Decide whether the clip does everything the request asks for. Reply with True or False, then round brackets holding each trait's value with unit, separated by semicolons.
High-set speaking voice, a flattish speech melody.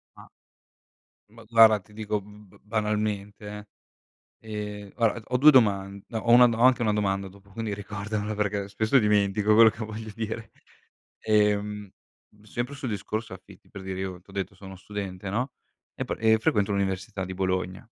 False (105 Hz; 2.0 semitones)